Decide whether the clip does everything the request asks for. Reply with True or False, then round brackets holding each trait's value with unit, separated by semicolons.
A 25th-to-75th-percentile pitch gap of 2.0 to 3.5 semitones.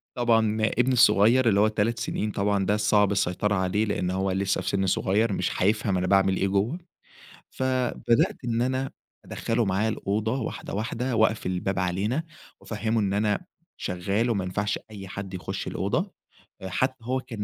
True (3.0 semitones)